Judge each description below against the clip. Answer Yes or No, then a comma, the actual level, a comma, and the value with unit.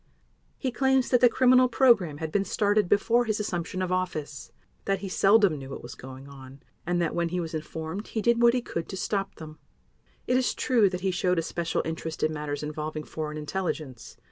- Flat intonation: No, wide, 5.5 semitones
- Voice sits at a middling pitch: Yes, medium, 180 Hz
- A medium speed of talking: No, fast, 210 wpm